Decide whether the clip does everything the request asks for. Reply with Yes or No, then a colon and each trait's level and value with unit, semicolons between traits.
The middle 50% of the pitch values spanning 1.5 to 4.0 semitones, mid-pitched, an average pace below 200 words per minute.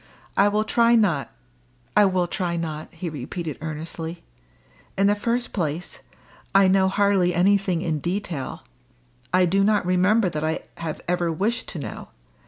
Yes: average, 3.6 semitones; medium, 180 Hz; average, 155 wpm